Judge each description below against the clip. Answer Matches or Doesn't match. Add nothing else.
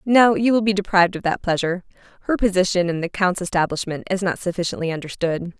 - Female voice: Matches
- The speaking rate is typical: Matches